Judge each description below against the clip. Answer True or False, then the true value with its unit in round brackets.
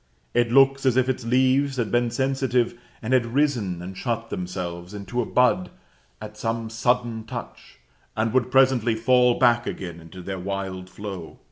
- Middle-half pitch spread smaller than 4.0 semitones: False (4.4 semitones)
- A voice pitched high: False (115 Hz)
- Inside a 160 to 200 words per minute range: True (165 wpm)